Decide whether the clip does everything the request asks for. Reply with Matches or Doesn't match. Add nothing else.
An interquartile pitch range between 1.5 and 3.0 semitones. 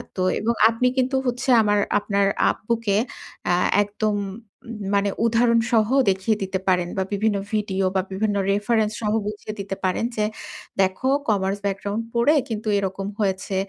Matches